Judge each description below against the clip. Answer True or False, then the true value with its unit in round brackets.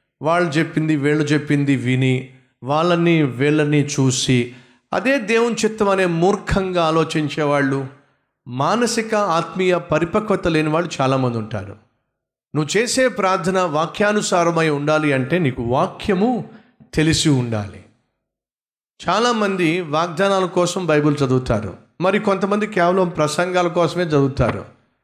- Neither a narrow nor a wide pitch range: False (5.7 semitones)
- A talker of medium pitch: True (160 Hz)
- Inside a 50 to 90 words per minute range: False (100 wpm)